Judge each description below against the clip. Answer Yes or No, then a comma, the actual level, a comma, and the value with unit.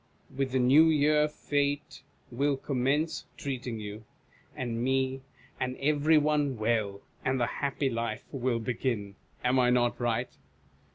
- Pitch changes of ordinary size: Yes, average, 3.2 semitones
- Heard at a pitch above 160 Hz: No, low, 130 Hz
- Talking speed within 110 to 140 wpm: Yes, slow, 135 wpm